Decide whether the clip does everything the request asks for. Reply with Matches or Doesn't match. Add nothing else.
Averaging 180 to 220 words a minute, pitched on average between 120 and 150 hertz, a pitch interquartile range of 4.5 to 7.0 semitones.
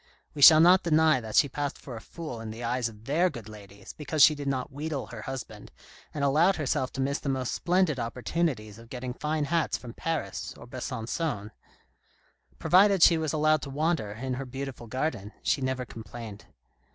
Matches